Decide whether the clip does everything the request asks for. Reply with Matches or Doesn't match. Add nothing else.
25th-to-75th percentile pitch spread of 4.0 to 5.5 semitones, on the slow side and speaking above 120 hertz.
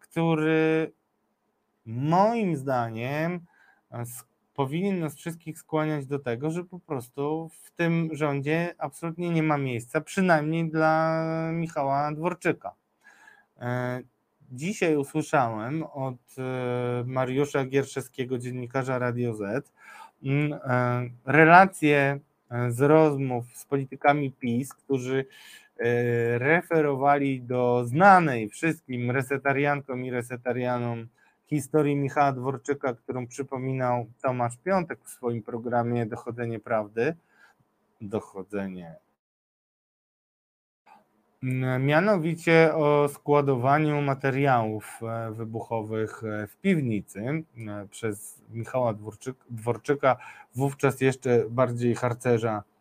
Matches